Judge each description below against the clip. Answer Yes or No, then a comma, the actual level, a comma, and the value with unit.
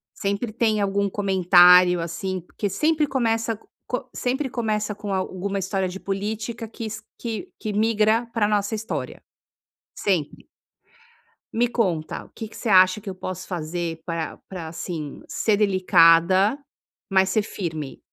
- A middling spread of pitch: Yes, average, 3.4 semitones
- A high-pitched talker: Yes, high, 200 Hz